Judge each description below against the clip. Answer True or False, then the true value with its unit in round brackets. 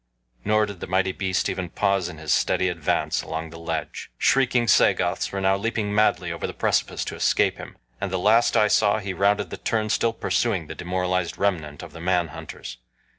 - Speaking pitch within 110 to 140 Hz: False (95 Hz)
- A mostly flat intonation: False (3.2 semitones)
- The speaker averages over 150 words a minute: True (200 wpm)